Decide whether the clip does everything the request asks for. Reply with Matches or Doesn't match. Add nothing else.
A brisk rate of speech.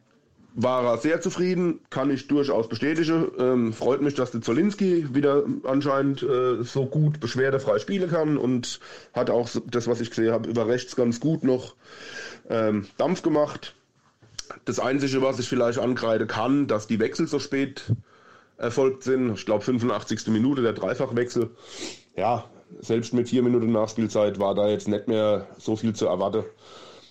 Doesn't match